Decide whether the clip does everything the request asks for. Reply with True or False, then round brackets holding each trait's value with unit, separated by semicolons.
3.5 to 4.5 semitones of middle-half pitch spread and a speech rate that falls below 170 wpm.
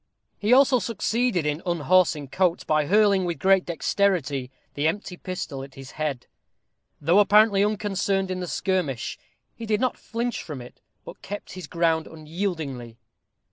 False (5.1 semitones; 150 wpm)